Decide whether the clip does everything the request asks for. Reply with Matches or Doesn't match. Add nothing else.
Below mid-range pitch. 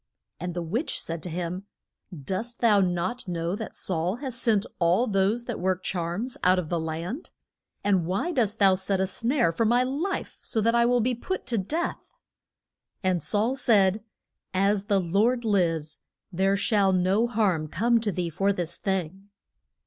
Doesn't match